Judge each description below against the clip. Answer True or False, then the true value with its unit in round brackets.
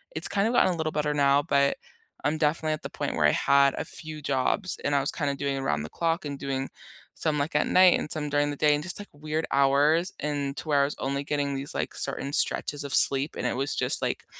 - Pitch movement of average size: False (1.8 semitones)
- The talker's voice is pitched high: False (145 Hz)